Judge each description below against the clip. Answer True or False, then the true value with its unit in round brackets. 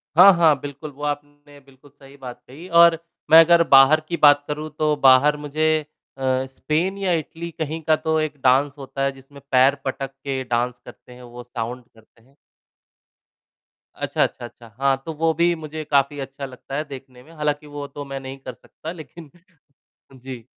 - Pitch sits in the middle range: True (145 Hz)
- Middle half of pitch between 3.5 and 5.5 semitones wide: False (2.7 semitones)